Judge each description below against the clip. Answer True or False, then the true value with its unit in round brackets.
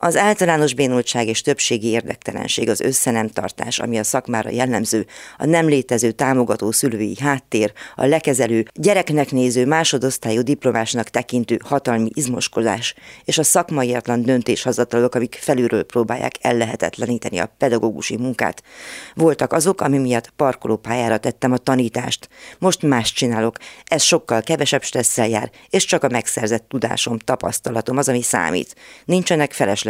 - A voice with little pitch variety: False (3.7 semitones)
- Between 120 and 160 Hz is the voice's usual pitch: True (125 Hz)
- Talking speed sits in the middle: True (130 wpm)